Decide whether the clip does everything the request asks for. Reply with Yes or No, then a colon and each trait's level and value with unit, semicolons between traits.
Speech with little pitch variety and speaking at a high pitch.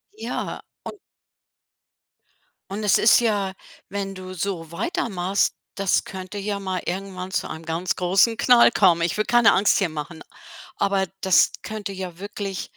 Yes: narrow, 2.1 semitones; high, 195 Hz